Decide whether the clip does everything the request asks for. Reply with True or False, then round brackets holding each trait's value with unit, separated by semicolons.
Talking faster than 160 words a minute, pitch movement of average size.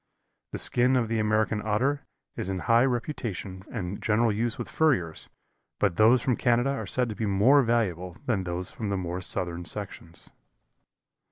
True (170 wpm; 4.6 semitones)